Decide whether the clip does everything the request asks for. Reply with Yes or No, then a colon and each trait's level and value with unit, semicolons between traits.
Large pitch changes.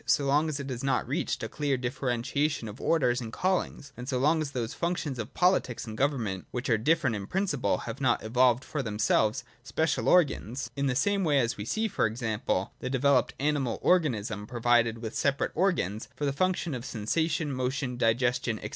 No: average, 4.2 semitones